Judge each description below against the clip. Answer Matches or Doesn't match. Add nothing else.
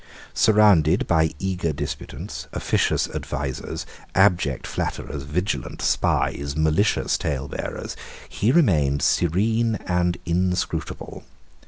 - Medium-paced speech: Doesn't match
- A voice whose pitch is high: Doesn't match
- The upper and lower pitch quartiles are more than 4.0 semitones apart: Matches